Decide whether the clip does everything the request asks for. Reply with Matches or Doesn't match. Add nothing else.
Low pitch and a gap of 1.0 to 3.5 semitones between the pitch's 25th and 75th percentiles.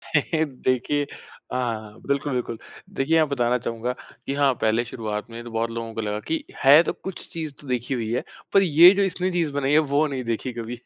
Doesn't match